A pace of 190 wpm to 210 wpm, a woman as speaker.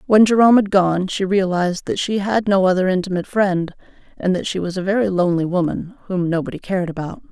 Yes: fast, 205 wpm; female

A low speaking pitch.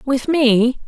No: very high, 260 Hz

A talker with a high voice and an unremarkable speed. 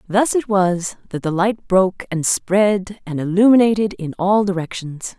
Yes: high, 195 Hz; average, 160 wpm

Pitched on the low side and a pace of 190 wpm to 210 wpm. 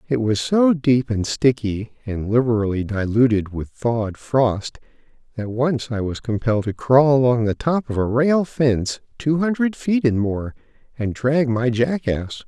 No: low, 125 Hz; average, 170 wpm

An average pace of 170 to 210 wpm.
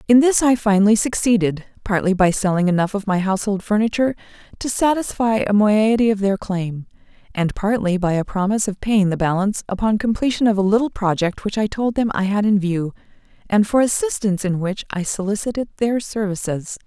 Yes: average, 180 wpm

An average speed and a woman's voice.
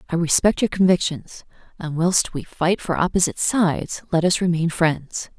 Yes: average, 165 wpm; female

